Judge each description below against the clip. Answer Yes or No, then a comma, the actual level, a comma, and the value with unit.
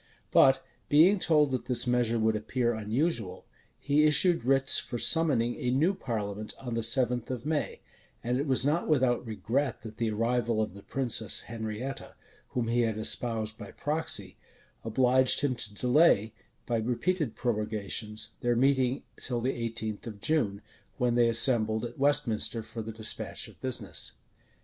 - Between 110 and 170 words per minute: Yes, average, 160 wpm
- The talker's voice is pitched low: Yes, low, 120 Hz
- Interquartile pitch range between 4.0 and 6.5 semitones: No, average, 3.3 semitones